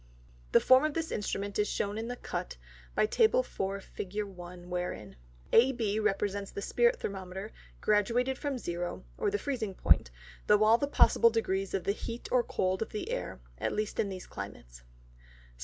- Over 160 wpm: Yes, average, 175 wpm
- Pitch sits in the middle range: No, high, 210 Hz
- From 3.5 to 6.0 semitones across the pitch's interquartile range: Yes, average, 4.1 semitones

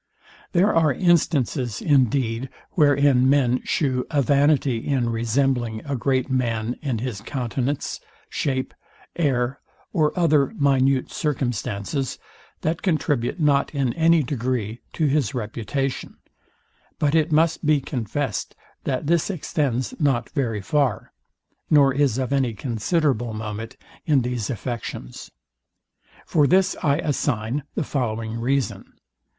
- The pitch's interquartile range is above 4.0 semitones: No, average, 3.6 semitones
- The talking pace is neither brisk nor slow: No, slow, 120 wpm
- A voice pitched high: No, low, 135 Hz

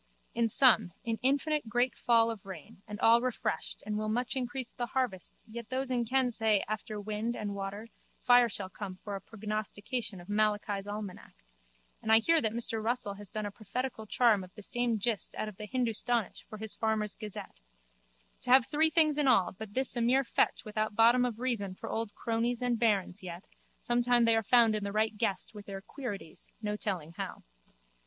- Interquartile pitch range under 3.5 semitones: Yes, average, 2.8 semitones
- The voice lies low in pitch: No, high, 220 Hz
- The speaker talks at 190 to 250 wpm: Yes, average, 200 wpm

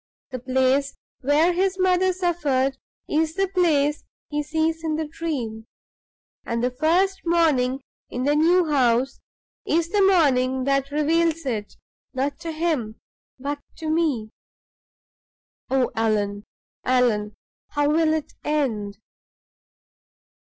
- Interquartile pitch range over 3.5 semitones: Yes, average, 4.4 semitones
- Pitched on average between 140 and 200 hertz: No, very high, 290 Hz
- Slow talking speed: Yes, slow, 120 wpm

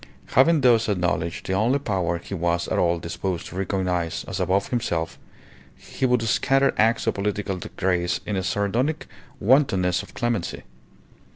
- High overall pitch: No, very low, 95 Hz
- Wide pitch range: No, average, 4.8 semitones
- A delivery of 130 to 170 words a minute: Yes, average, 155 wpm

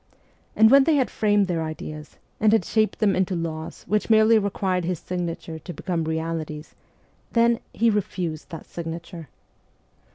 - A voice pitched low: No, medium, 180 Hz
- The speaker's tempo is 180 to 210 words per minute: No, average, 155 wpm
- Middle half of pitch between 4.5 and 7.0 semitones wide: Yes, average, 4.8 semitones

